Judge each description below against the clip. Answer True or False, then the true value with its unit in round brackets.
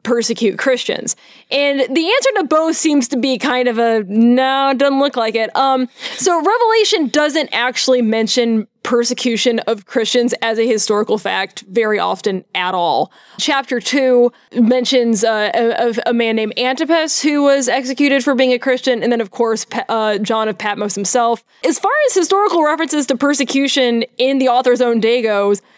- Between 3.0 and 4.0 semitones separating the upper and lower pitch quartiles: True (3.4 semitones)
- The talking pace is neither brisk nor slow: True (170 wpm)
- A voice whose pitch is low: False (245 Hz)